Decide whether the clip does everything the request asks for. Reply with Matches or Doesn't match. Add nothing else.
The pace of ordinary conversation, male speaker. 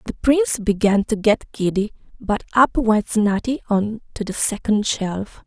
Doesn't match